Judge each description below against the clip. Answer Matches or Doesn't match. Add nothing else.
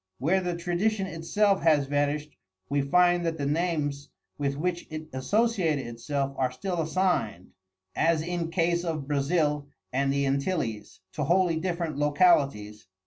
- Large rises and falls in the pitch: Doesn't match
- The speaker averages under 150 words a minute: Matches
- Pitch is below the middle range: Doesn't match